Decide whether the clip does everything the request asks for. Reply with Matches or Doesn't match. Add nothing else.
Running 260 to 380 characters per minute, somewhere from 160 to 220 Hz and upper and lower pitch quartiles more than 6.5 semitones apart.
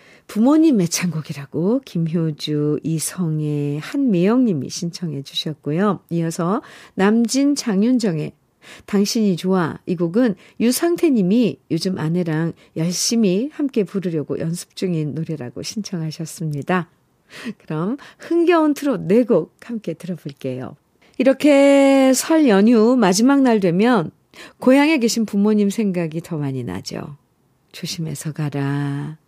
Matches